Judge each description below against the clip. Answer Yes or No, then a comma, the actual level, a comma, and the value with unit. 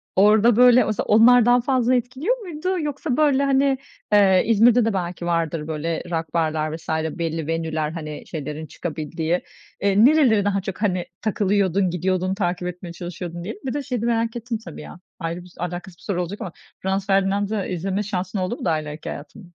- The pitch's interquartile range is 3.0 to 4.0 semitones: No, wide, 5.4 semitones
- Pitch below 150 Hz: No, high, 190 Hz